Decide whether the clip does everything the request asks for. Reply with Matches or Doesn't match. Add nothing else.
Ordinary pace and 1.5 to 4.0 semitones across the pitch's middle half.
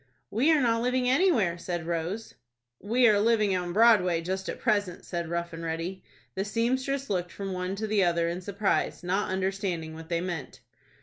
Doesn't match